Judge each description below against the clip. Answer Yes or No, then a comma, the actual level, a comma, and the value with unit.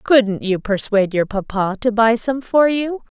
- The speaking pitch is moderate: No, high, 225 Hz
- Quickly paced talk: No, average, 190 wpm